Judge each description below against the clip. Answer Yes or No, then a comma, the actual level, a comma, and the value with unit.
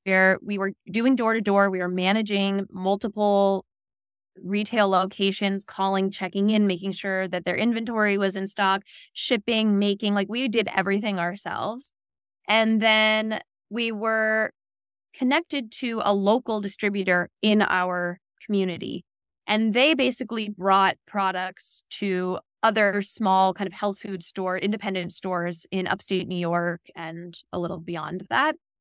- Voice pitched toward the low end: No, high, 195 Hz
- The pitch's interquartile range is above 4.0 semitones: No, narrow, 2.6 semitones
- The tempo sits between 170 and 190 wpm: No, average, 140 wpm